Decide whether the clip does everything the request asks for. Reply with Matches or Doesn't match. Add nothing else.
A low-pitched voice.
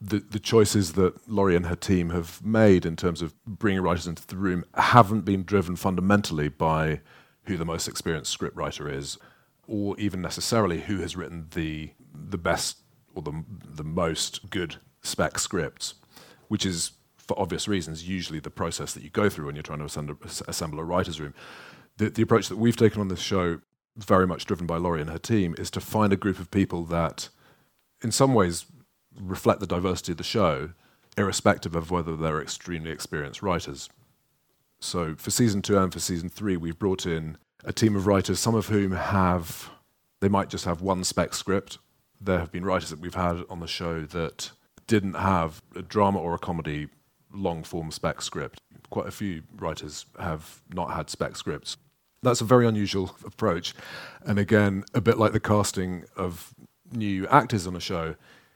Matches